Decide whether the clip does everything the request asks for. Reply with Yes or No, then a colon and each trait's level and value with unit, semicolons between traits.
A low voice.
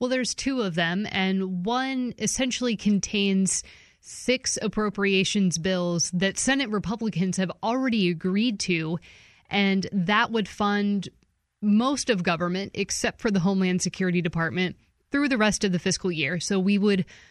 No: high, 195 Hz